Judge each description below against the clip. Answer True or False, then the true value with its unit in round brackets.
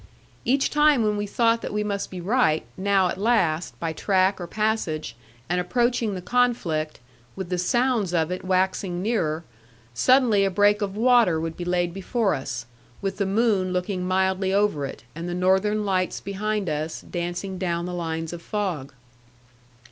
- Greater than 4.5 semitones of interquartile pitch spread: False (3.4 semitones)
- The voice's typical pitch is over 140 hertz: True (190 Hz)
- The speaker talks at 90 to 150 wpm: False (170 wpm)